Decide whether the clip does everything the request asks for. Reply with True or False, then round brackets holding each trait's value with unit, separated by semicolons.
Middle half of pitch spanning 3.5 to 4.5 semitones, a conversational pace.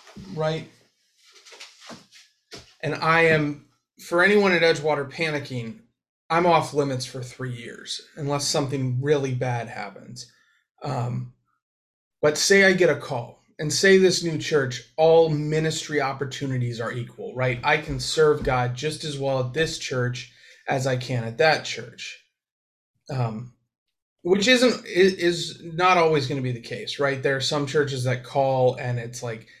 True (4.1 semitones; 150 wpm)